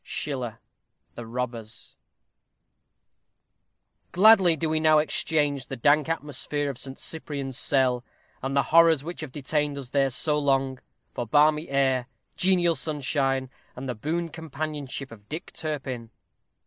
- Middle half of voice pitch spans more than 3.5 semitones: No, average, 2.9 semitones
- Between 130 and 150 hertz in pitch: Yes, medium, 140 Hz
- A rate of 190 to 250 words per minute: No, slow, 135 wpm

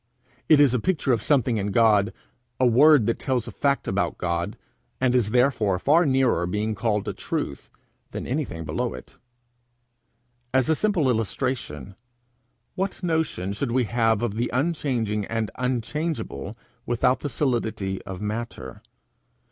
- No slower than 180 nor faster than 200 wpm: No, average, 150 wpm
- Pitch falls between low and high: No, low, 120 Hz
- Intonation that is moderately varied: Yes, average, 4.6 semitones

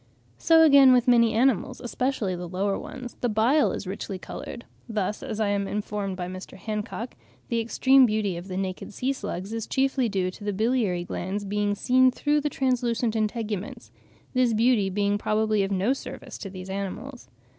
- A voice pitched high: Yes, high, 215 Hz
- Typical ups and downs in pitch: Yes, average, 4.2 semitones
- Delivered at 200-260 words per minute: No, average, 180 wpm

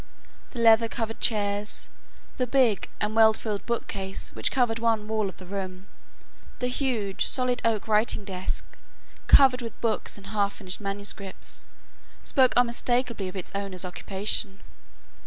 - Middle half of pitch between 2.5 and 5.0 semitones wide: Yes, average, 3.1 semitones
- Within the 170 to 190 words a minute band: No, average, 140 wpm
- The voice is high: Yes, high, 215 Hz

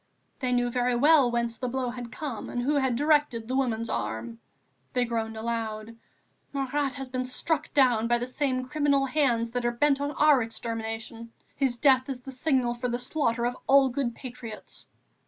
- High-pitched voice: Yes, very high, 250 Hz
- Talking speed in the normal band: Yes, average, 185 wpm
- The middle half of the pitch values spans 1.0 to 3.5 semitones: Yes, average, 2.8 semitones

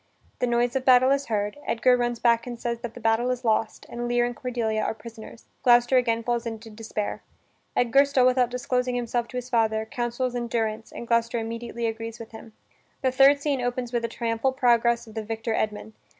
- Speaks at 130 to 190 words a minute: No, fast, 205 wpm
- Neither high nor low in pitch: No, high, 235 Hz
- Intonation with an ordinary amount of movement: No, narrow, 1.6 semitones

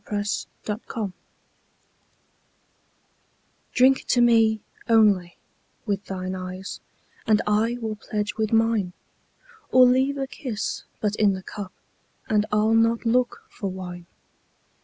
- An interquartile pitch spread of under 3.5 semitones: Yes, narrow, 2.6 semitones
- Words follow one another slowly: Yes, slow, 125 wpm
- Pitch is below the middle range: No, high, 215 Hz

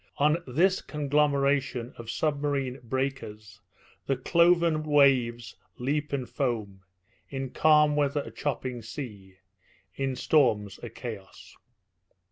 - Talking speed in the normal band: No, slow, 105 wpm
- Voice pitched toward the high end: No, low, 135 Hz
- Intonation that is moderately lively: Yes, average, 3.8 semitones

